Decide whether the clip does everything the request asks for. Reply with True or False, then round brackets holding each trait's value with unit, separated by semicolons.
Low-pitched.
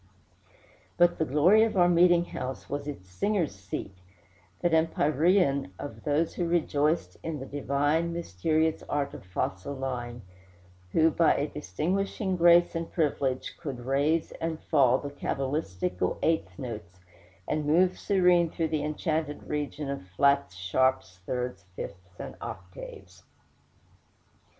False (145 Hz)